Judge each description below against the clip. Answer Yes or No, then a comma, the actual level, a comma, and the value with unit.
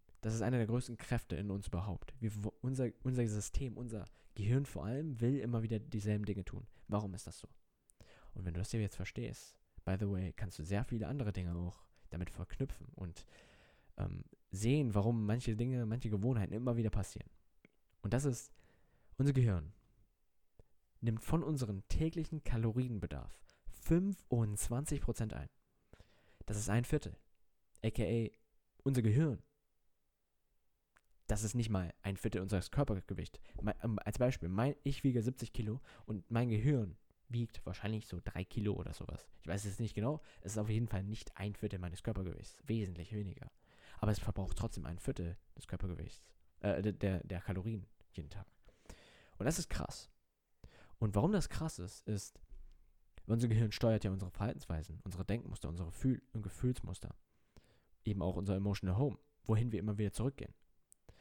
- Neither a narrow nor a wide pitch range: Yes, average, 3.8 semitones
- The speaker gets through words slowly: No, average, 160 wpm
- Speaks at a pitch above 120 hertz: No, low, 105 Hz